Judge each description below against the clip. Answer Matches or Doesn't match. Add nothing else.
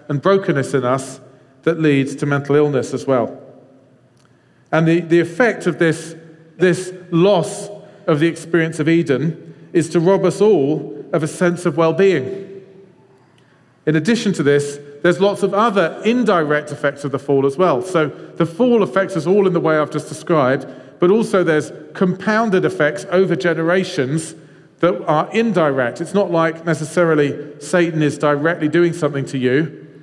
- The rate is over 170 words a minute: Doesn't match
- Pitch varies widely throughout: Doesn't match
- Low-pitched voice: Doesn't match